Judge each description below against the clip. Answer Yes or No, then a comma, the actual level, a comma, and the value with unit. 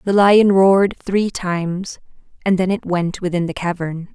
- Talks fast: No, average, 175 wpm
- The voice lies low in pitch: No, medium, 185 Hz